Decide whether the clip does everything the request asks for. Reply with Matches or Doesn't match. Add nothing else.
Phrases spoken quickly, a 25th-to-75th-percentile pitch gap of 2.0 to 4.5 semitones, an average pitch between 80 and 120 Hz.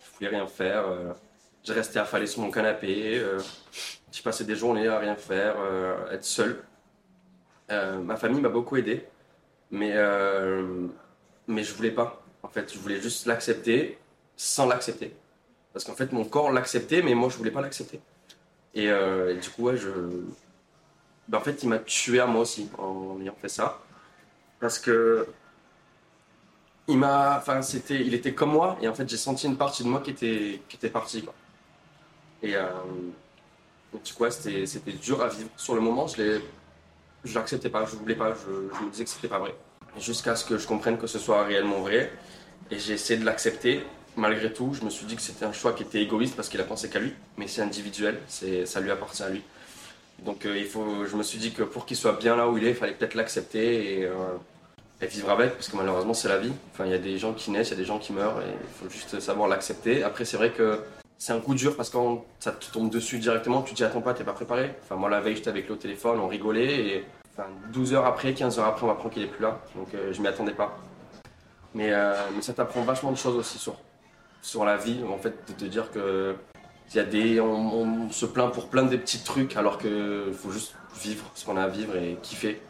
Matches